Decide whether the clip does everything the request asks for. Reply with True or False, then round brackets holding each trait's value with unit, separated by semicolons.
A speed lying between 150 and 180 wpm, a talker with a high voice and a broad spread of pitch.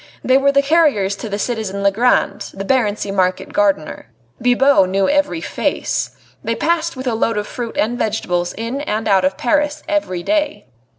True (170 wpm; 225 Hz; 6.0 semitones)